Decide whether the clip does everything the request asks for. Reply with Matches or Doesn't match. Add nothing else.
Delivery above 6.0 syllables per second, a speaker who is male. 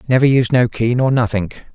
Doesn't match